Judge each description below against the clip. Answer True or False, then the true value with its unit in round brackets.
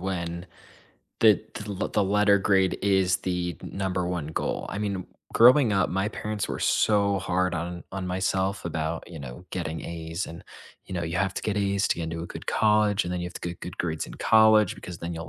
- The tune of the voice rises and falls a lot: False (2.7 semitones)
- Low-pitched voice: True (95 Hz)